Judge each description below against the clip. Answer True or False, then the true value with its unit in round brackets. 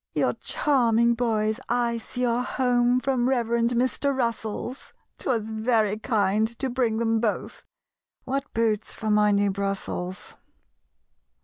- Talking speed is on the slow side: True (125 wpm)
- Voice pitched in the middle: False (230 Hz)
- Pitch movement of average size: False (2.3 semitones)